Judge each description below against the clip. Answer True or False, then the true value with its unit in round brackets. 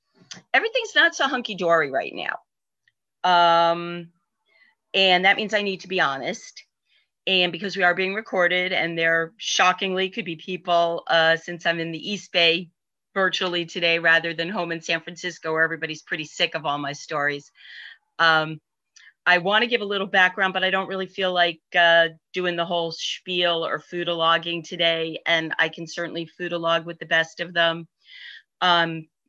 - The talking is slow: False (175 wpm)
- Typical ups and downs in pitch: False (2.1 semitones)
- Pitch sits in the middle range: True (170 Hz)